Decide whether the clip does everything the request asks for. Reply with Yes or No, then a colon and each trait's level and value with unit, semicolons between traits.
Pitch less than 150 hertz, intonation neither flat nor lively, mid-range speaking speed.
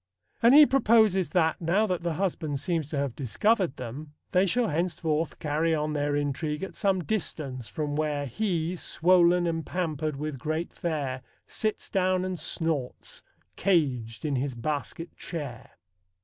No: medium, 160 Hz; average, 4.0 semitones; average, 150 wpm